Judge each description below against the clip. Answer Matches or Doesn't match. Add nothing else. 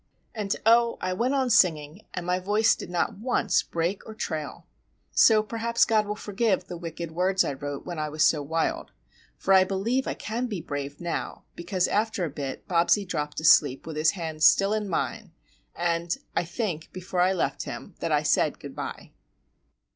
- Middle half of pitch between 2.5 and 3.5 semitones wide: Doesn't match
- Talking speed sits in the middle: Matches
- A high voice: Doesn't match